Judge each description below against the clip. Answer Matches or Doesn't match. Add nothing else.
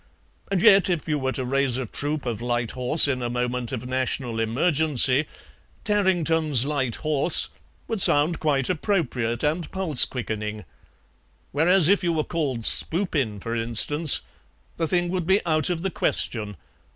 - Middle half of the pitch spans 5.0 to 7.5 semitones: Matches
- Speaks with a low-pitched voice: Doesn't match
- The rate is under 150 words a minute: Doesn't match